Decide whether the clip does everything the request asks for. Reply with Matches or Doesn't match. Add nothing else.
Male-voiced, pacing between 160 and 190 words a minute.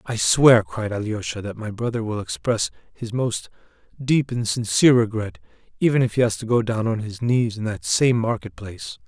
Doesn't match